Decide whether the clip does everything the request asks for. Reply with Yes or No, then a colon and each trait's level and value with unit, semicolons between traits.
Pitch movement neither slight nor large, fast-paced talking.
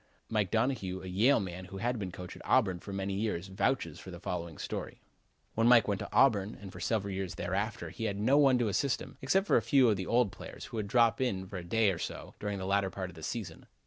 Yes: average, 3.8 semitones; fast, 255 wpm